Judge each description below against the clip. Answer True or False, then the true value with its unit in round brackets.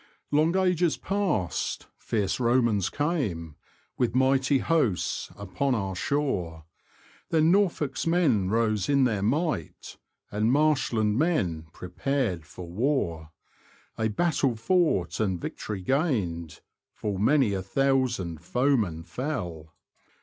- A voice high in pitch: False (115 Hz)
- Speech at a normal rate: False (110 wpm)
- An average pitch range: False (7.7 semitones)